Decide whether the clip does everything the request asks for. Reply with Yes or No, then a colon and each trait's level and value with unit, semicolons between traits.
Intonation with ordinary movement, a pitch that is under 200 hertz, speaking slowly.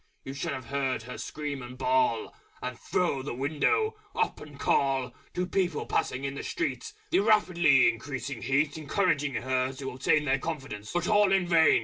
No: average, 4.9 semitones; medium, 140 Hz; average, 175 wpm